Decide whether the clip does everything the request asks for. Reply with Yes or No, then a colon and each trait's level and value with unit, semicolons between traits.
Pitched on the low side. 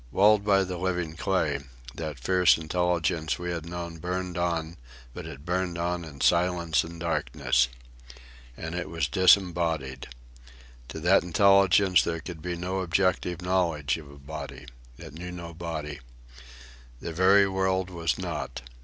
Yes: very low, 85 Hz